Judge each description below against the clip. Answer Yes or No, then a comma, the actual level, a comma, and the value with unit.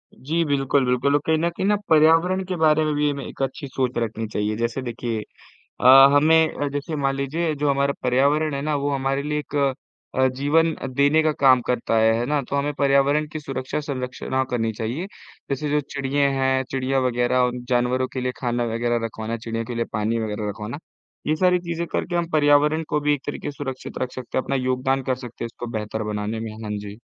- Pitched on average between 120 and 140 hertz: Yes, low, 135 Hz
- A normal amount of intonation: Yes, average, 3.4 semitones